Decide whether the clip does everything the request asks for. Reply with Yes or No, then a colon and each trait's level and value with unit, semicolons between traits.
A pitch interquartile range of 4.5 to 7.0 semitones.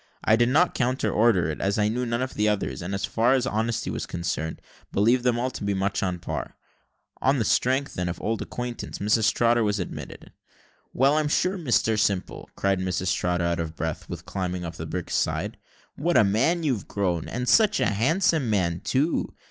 Yes: wide, 5.5 semitones